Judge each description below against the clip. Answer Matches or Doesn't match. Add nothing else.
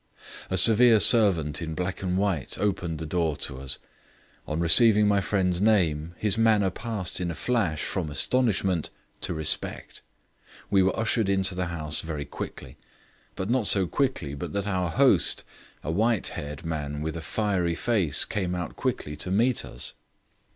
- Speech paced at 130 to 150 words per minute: Doesn't match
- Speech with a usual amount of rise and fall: Matches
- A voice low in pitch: Matches